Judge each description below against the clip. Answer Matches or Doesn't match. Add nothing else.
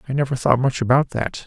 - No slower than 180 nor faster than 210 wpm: Doesn't match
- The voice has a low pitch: Matches